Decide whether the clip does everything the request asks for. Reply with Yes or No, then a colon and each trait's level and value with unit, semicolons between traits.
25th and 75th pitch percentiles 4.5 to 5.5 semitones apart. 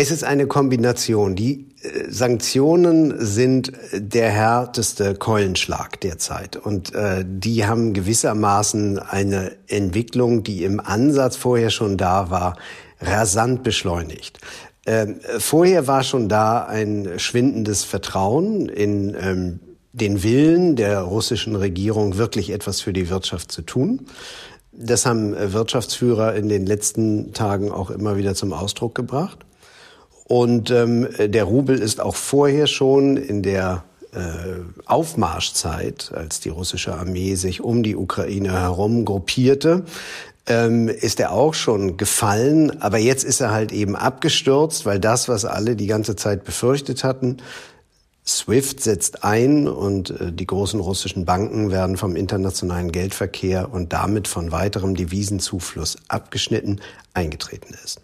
No: average, 4.0 semitones